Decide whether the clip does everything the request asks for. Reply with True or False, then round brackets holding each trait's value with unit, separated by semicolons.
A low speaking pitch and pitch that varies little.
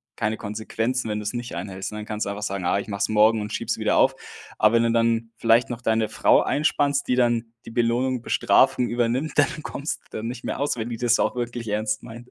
True (115 Hz; 2.1 semitones)